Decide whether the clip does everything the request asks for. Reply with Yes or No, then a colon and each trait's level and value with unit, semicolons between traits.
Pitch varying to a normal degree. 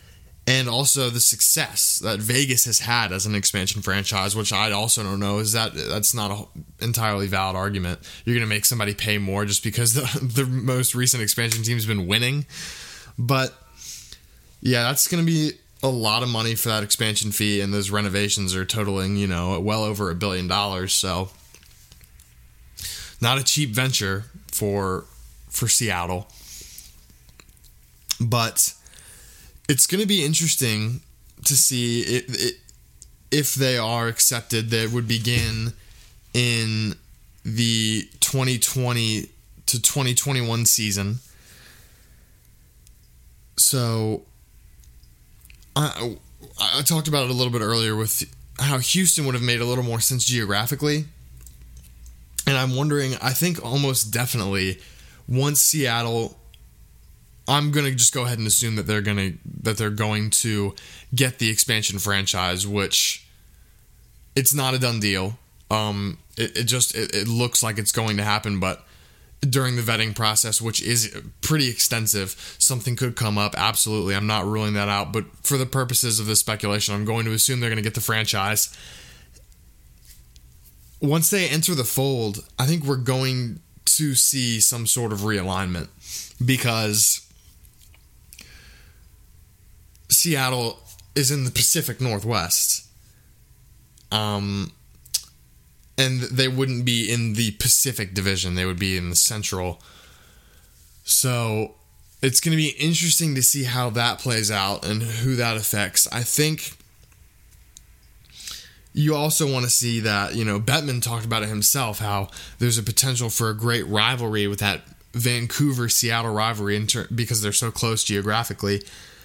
Yes: average, 4.1 semitones